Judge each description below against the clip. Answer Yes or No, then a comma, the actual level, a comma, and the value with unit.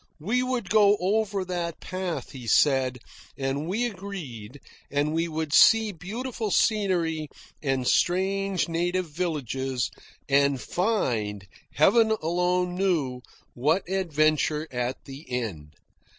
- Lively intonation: Yes, wide, 6.1 semitones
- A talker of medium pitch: Yes, medium, 165 Hz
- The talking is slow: Yes, slow, 115 wpm